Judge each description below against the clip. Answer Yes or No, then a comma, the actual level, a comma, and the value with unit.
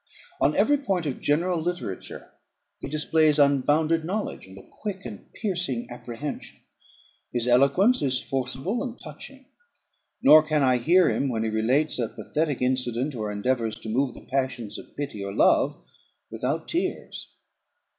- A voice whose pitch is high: No, medium, 140 Hz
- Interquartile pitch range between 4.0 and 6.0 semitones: Yes, average, 5.1 semitones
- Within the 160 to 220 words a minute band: No, average, 150 wpm